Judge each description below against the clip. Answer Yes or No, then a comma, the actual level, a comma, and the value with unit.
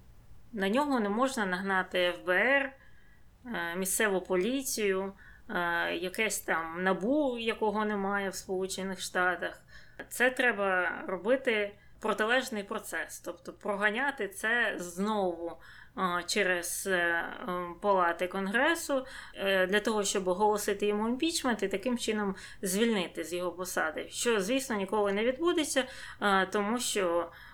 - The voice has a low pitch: No, high, 205 Hz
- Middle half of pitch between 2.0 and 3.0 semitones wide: No, average, 3.9 semitones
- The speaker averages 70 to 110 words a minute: Yes, slow, 105 wpm